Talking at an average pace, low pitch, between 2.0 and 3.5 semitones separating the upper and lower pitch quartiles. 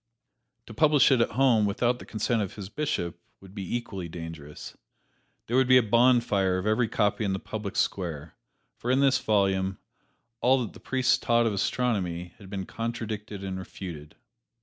No: average, 175 wpm; low, 105 Hz; average, 4.2 semitones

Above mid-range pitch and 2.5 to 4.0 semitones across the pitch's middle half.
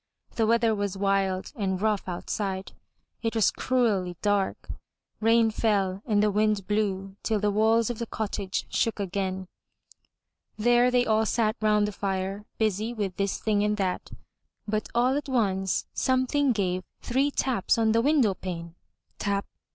Yes: high, 210 Hz; average, 2.8 semitones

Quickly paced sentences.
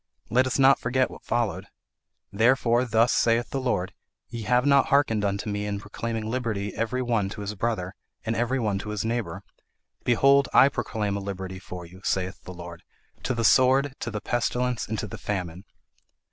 No: average, 190 wpm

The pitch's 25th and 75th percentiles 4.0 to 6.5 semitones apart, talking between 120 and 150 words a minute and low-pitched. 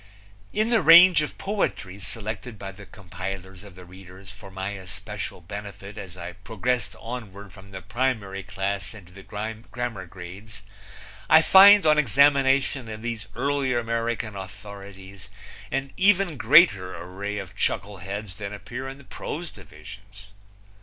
Yes: average, 4.6 semitones; average, 140 wpm; low, 105 Hz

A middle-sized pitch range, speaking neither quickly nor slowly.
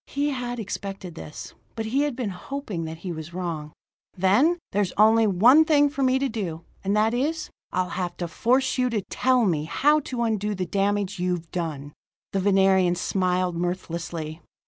No: wide, 5.9 semitones; average, 180 wpm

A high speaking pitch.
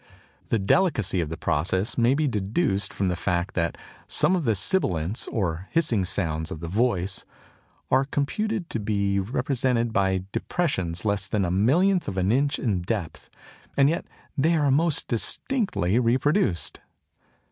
No: low, 110 Hz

